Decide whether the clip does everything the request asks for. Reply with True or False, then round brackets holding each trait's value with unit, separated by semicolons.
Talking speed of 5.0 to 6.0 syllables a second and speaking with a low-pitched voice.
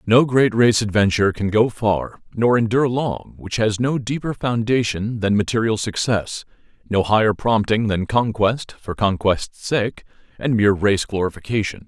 False (4.7 syllables/s; 110 Hz)